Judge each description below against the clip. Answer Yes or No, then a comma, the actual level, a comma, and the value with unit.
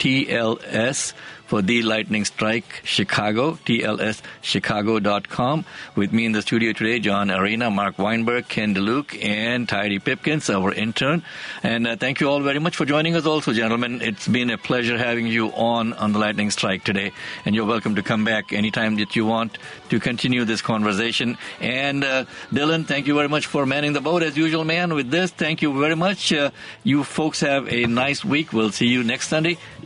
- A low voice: Yes, low, 120 Hz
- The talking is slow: No, average, 190 wpm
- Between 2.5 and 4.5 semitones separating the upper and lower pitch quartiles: No, average, 5.0 semitones